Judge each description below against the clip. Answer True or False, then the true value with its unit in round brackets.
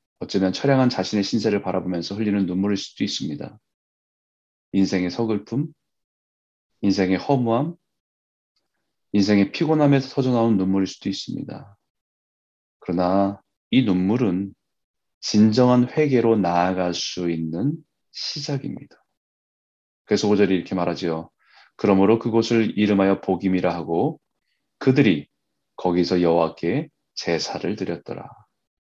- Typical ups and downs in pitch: True (4.4 semitones)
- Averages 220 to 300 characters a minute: True (275 characters per minute)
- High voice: False (100 Hz)